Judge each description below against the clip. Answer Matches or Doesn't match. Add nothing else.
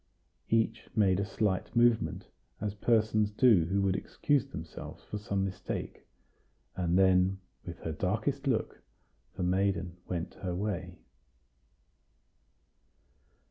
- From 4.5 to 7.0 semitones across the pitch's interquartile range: Doesn't match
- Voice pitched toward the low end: Matches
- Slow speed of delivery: Matches